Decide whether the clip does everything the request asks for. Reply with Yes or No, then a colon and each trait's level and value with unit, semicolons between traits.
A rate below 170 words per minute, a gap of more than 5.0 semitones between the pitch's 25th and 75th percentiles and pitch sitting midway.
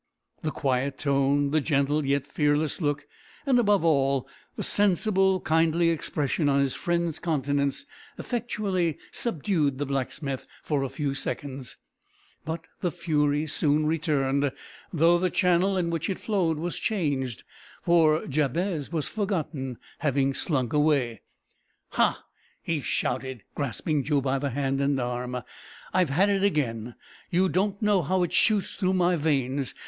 No: average, 145 wpm; average, 4.0 semitones; medium, 150 Hz